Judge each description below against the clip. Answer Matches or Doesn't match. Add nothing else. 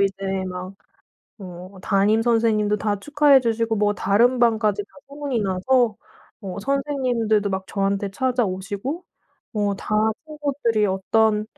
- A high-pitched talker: Matches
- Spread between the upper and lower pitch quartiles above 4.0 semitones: Doesn't match